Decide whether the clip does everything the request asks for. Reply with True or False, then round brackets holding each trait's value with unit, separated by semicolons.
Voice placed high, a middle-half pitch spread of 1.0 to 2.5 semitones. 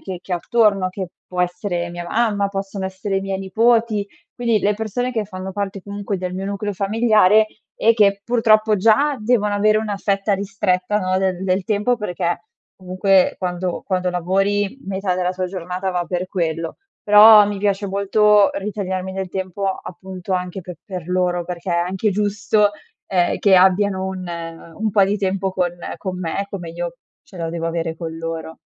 True (195 Hz; 2.2 semitones)